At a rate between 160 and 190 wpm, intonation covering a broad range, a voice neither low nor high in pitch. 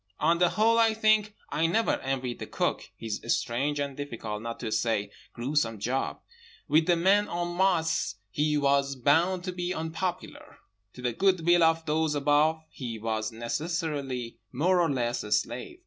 Yes: average, 170 wpm; wide, 6.2 semitones; medium, 150 Hz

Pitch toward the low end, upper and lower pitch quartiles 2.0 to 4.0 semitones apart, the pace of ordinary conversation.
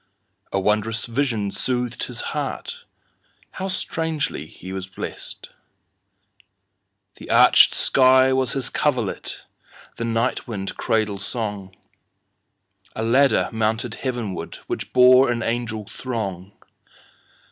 No: low, 115 Hz; average, 3.5 semitones; slow, 90 wpm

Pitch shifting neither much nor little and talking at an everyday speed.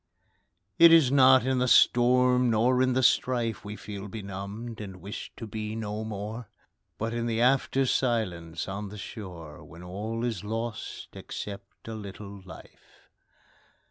Yes: average, 3.6 semitones; average, 150 wpm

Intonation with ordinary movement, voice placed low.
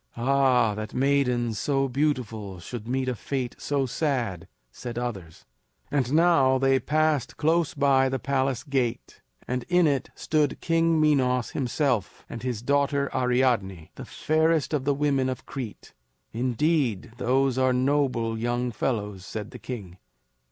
Yes: average, 3.1 semitones; low, 130 Hz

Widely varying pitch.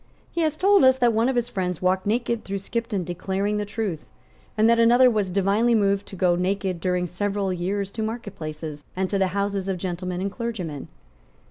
No: average, 3.8 semitones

